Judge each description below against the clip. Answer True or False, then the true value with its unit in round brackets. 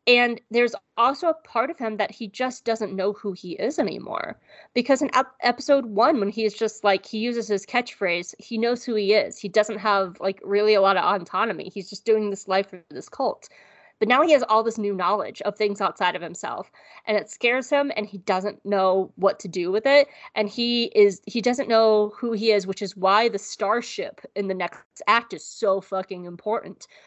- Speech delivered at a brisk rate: True (215 wpm)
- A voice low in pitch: False (210 Hz)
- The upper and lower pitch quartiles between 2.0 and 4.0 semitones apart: True (3.4 semitones)